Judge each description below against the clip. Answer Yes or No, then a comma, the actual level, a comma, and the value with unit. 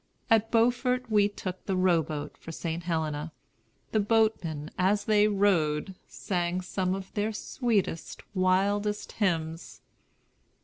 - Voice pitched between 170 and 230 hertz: Yes, high, 190 Hz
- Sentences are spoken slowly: Yes, slow, 125 wpm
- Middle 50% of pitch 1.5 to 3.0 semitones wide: No, average, 4.0 semitones